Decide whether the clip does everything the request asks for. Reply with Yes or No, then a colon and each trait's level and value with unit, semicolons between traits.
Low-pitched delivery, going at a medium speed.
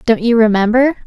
No: high, 230 Hz; average, 170 wpm